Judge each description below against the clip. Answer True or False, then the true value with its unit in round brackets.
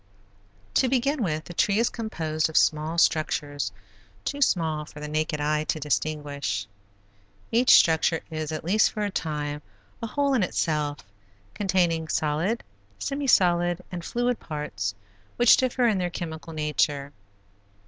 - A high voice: False (160 Hz)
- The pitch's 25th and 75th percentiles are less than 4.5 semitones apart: False (5.4 semitones)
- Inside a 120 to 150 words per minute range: True (145 wpm)